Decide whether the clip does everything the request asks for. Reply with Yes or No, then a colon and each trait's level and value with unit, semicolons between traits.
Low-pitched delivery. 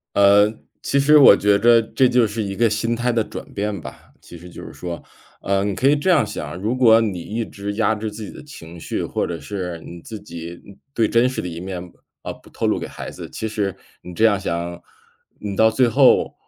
Yes: low, 105 Hz